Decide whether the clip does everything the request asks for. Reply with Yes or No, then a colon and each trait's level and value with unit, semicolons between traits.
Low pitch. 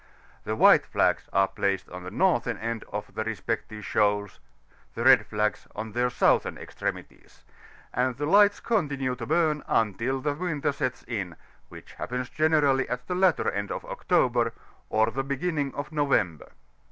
Yes: low, 125 Hz